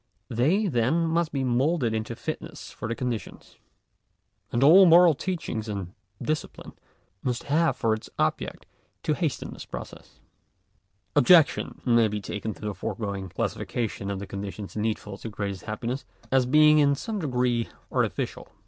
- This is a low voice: Yes, low, 120 Hz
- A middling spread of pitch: No, wide, 6.1 semitones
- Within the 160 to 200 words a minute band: No, average, 150 wpm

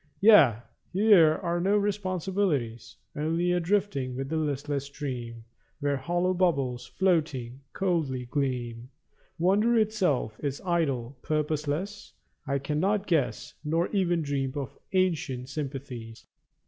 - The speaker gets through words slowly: Yes, slow, 115 wpm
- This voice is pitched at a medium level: Yes, medium, 150 Hz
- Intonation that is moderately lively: No, wide, 5.7 semitones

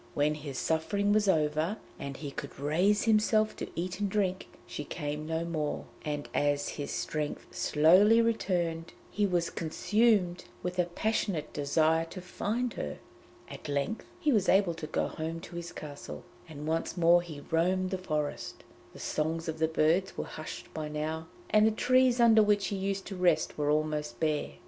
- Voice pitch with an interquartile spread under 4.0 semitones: No, average, 4.6 semitones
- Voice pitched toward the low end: No, medium, 170 Hz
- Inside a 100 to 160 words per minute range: No, average, 180 wpm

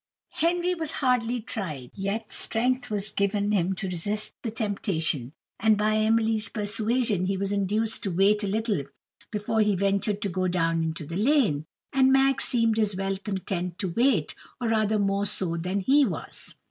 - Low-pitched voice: No, high, 205 Hz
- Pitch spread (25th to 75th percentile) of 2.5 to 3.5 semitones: Yes, average, 3.0 semitones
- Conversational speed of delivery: Yes, average, 170 wpm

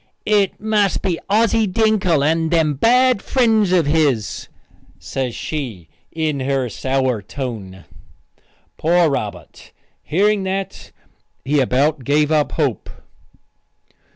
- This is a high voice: No, medium, 155 Hz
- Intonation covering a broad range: Yes, wide, 6.7 semitones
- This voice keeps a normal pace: No, slow, 110 wpm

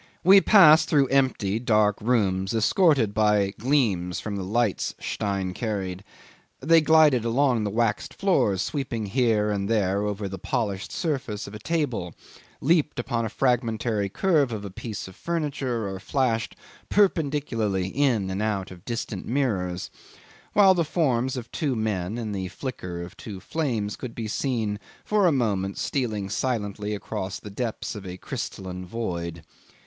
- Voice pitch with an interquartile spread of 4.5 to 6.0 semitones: Yes, average, 5.1 semitones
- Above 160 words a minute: No, average, 155 wpm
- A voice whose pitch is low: Yes, low, 110 Hz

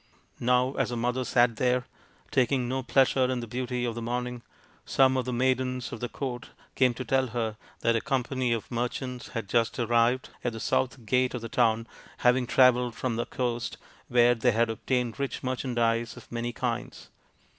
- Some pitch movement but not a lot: No, narrow, 1.5 semitones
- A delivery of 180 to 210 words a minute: Yes, average, 190 wpm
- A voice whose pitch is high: No, low, 125 Hz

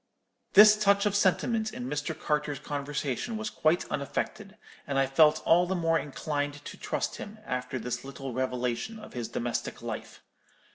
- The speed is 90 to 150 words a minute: No, average, 160 wpm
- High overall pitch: No, medium, 150 Hz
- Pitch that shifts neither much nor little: No, wide, 7.0 semitones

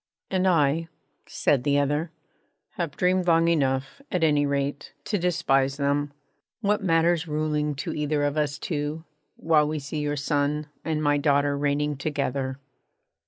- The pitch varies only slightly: Yes, narrow, 2.3 semitones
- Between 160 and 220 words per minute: No, average, 150 wpm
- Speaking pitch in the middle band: Yes, medium, 150 Hz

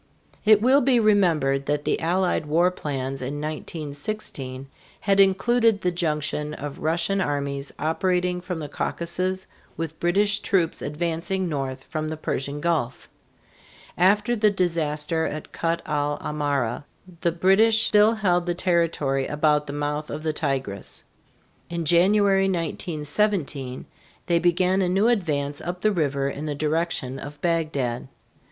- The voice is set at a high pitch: No, medium, 165 Hz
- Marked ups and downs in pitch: No, average, 4.3 semitones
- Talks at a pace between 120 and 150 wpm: Yes, average, 140 wpm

